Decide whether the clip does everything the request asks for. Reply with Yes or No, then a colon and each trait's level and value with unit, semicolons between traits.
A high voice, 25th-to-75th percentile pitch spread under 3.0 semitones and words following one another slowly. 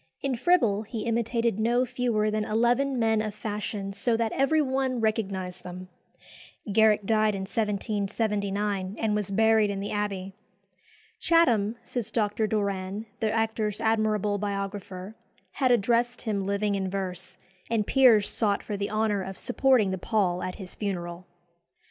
No: high, 210 Hz; narrow, 2.4 semitones; average, 150 wpm